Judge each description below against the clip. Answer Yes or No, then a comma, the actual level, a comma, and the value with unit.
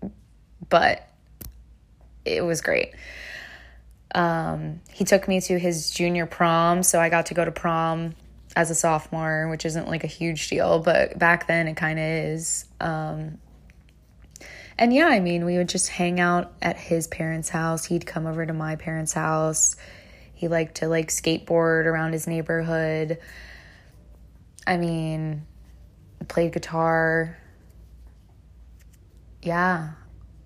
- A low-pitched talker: No, medium, 160 Hz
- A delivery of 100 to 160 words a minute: Yes, slow, 135 wpm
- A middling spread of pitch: No, narrow, 1.9 semitones